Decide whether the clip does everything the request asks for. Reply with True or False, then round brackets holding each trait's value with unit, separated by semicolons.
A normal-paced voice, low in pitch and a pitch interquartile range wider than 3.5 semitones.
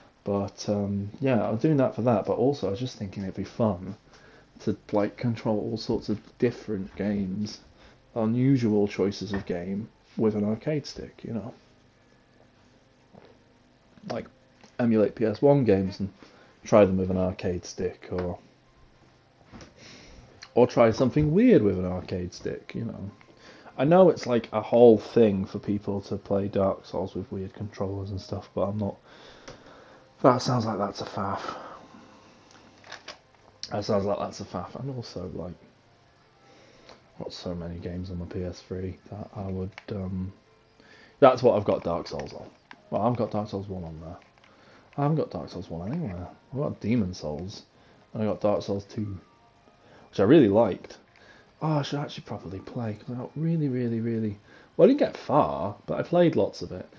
True (170 wpm; 105 Hz; 3.9 semitones)